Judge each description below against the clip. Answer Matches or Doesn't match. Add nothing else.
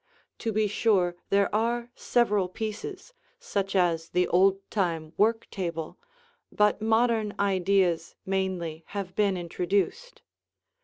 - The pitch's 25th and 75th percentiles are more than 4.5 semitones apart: Doesn't match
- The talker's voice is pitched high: Matches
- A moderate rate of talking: Doesn't match